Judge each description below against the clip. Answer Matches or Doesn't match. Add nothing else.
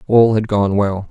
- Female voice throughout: Doesn't match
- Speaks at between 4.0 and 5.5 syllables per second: Matches